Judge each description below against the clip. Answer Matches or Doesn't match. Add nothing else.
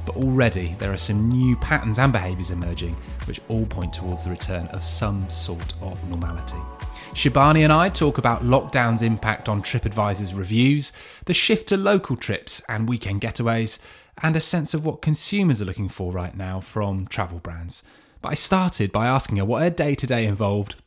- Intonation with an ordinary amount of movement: Doesn't match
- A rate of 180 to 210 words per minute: Matches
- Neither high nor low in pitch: Doesn't match